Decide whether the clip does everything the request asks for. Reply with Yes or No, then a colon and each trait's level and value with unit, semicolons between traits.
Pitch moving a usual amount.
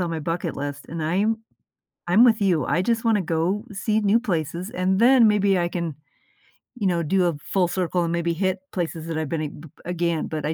Yes: average, 3.5 semitones